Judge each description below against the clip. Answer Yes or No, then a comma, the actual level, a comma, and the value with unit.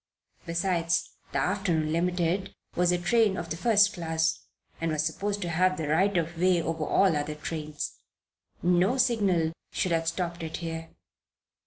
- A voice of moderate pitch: Yes, medium, 170 Hz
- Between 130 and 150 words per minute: No, average, 160 wpm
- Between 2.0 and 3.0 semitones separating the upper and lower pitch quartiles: Yes, narrow, 2.4 semitones